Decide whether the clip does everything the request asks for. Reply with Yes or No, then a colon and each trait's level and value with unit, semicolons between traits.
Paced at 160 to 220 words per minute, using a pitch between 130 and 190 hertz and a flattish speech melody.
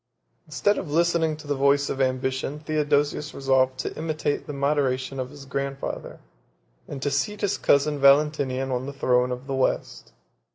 Yes: average, 165 wpm; medium, 140 Hz; narrow, 2.2 semitones